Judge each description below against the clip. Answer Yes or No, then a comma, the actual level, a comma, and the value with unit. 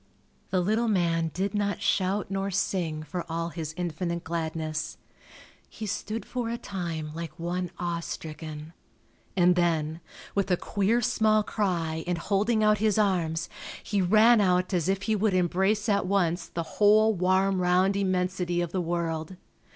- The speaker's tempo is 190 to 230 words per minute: No, average, 160 wpm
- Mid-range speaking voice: Yes, medium, 180 Hz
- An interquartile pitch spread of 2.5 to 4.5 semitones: Yes, average, 3.2 semitones